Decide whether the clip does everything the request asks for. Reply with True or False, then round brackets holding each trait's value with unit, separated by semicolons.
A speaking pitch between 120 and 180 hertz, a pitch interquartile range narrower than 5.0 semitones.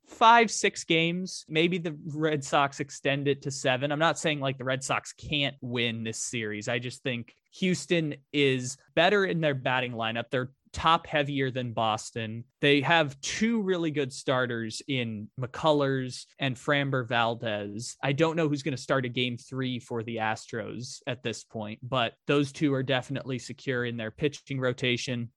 True (135 Hz; 3.6 semitones)